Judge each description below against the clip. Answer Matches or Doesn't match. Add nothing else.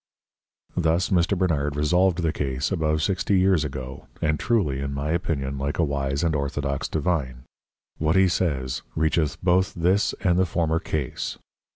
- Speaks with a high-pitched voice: Doesn't match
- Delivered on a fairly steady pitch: Doesn't match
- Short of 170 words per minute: Matches